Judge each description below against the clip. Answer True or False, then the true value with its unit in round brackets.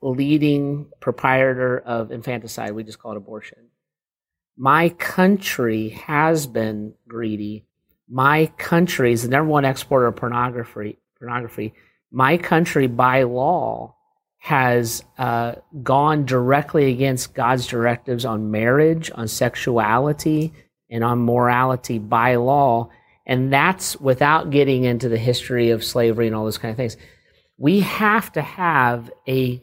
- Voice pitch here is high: False (125 Hz)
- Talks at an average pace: False (130 wpm)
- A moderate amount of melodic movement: True (3.6 semitones)